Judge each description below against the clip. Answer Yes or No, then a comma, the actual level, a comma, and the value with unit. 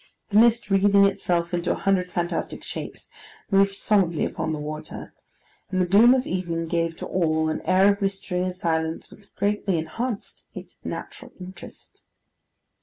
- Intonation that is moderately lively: Yes, average, 3.0 semitones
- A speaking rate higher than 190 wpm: No, average, 160 wpm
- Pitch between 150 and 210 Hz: Yes, medium, 185 Hz